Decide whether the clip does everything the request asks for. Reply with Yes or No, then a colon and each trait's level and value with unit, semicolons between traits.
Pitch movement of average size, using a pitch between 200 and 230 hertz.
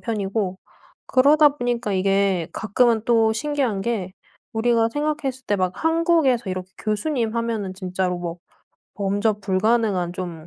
Yes: average, 4.3 semitones; high, 220 Hz